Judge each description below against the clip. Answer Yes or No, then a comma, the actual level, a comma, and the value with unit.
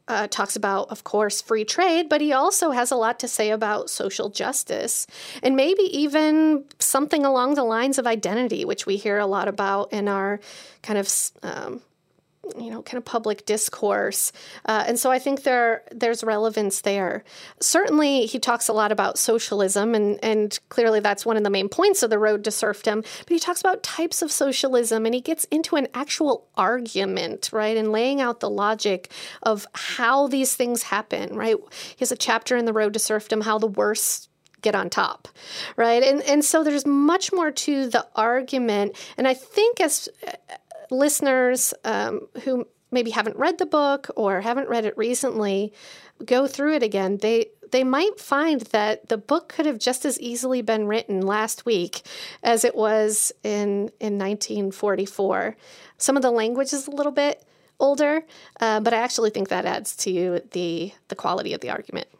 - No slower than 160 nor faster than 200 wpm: Yes, average, 185 wpm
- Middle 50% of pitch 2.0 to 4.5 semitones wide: No, average, 5.0 semitones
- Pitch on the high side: Yes, high, 240 Hz